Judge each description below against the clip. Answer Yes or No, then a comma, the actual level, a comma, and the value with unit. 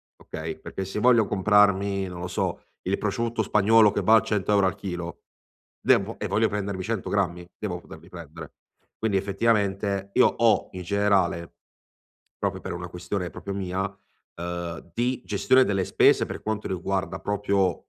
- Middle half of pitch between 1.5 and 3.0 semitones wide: Yes, narrow, 2.6 semitones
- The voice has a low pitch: Yes, low, 100 Hz